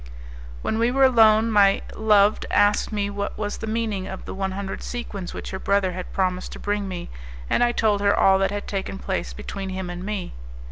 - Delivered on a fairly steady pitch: Yes, narrow, 2.0 semitones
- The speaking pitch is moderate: No, high, 200 Hz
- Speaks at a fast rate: Yes, fast, 215 wpm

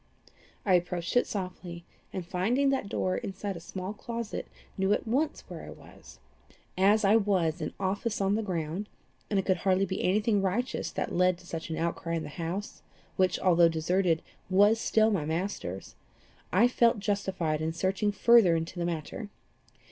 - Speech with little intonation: No, average, 3.3 semitones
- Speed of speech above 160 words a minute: Yes, average, 180 wpm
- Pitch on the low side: No, high, 190 Hz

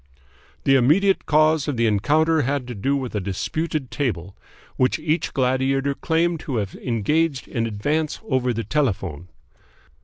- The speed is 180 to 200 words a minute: No, average, 150 wpm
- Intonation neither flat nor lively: Yes, average, 5.0 semitones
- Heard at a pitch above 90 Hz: Yes, low, 135 Hz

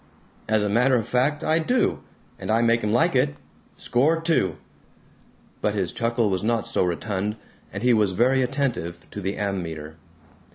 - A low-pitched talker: Yes, low, 110 Hz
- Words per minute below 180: Yes, average, 170 wpm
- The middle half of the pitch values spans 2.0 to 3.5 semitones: No, average, 4.6 semitones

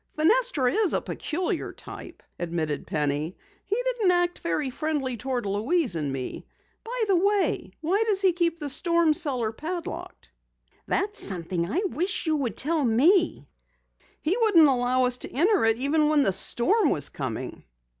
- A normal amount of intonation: No, wide, 8.2 semitones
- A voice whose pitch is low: No, very high, 305 Hz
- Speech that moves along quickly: No, average, 160 wpm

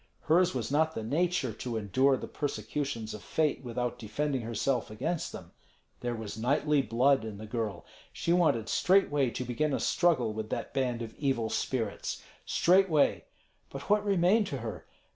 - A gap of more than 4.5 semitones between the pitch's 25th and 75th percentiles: Yes, average, 5.3 semitones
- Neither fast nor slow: Yes, average, 165 wpm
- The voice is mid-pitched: No, low, 130 Hz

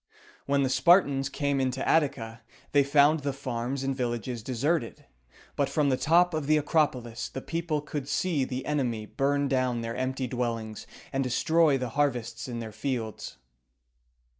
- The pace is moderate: Yes, average, 160 wpm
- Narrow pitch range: No, average, 3.1 semitones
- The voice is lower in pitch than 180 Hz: Yes, low, 135 Hz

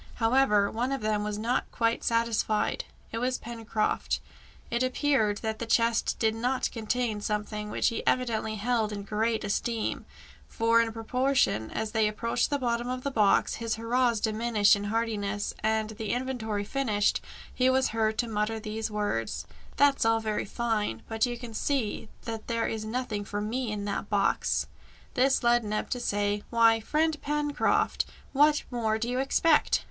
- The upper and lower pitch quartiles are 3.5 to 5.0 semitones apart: No, narrow, 2.5 semitones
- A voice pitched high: Yes, high, 225 Hz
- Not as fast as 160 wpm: No, average, 170 wpm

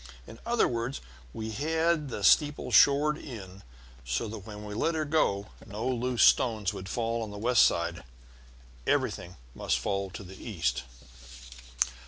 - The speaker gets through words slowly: No, average, 155 wpm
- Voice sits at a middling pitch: No, low, 110 Hz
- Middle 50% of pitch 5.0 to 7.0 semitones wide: Yes, wide, 5.6 semitones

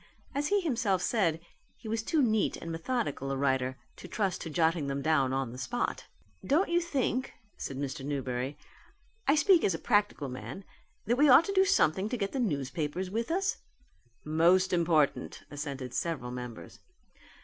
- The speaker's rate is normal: Yes, average, 170 wpm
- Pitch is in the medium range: Yes, medium, 170 Hz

